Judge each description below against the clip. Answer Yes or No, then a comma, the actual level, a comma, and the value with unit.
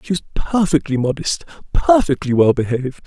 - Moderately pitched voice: Yes, medium, 150 Hz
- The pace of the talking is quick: No, slow, 135 wpm